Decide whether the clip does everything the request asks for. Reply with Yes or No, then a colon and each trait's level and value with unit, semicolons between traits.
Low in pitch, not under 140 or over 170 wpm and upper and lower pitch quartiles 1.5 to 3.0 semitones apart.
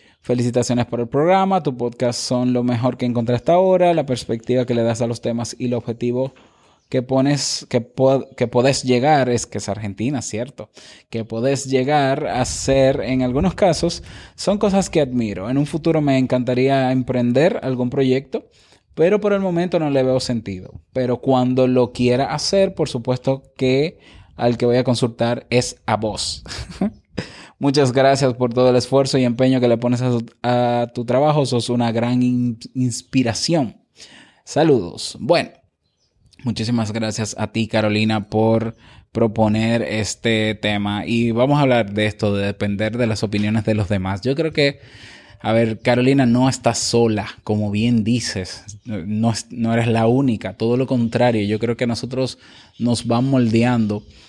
Yes: low, 120 Hz; average, 165 wpm; narrow, 2.6 semitones